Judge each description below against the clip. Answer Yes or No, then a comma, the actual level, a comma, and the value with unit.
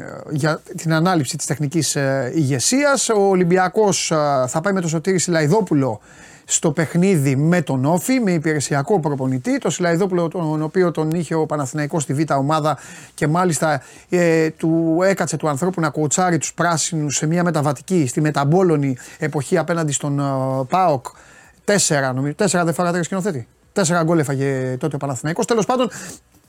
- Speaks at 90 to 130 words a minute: No, average, 165 wpm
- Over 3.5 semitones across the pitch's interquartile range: No, average, 3.2 semitones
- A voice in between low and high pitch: Yes, medium, 160 Hz